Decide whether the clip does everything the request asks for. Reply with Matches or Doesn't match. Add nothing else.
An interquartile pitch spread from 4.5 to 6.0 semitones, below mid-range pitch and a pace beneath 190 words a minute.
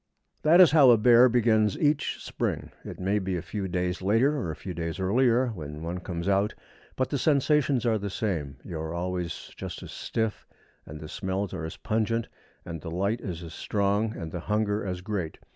Doesn't match